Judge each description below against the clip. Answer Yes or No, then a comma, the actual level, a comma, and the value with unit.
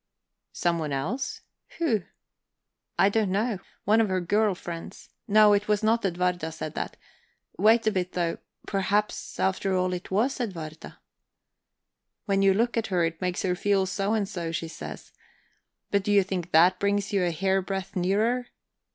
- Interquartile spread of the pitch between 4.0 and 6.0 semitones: No, average, 2.8 semitones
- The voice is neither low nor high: No, high, 195 Hz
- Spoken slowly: No, average, 165 wpm